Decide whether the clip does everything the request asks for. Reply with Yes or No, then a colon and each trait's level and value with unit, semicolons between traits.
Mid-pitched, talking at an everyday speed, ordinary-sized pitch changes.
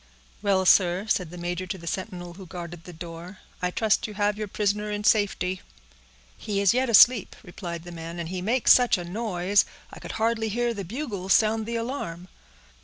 No: high, 195 Hz; average, 195 wpm; average, 3.6 semitones